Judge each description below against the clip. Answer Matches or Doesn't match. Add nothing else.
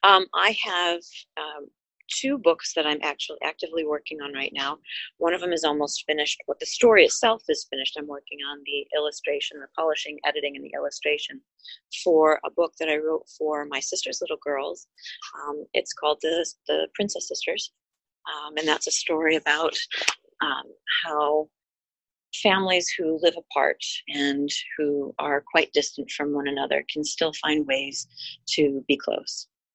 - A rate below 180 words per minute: Matches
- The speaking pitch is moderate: Matches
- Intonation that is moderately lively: Matches